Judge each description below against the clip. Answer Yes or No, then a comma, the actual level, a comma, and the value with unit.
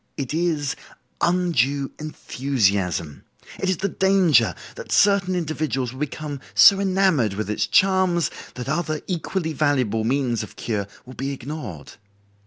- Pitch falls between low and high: Yes, medium, 145 Hz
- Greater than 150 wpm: No, slow, 135 wpm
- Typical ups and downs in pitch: No, wide, 6.2 semitones